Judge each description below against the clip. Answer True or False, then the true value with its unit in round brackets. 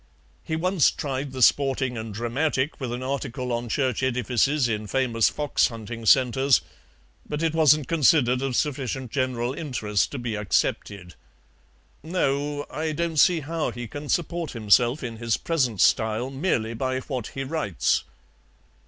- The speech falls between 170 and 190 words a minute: False (150 wpm)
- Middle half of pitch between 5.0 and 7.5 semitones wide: False (3.8 semitones)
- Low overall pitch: True (130 Hz)